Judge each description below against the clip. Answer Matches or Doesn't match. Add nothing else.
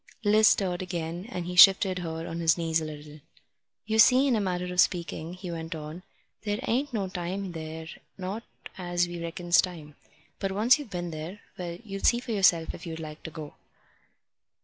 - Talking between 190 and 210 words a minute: Matches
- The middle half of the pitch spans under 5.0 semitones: Matches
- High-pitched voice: Doesn't match